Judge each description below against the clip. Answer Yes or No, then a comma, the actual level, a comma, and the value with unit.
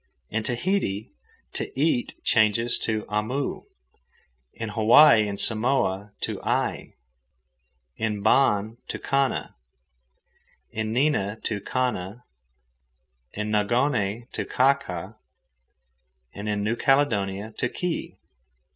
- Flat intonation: No, average, 3.6 semitones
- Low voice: Yes, low, 110 Hz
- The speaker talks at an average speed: No, slow, 100 wpm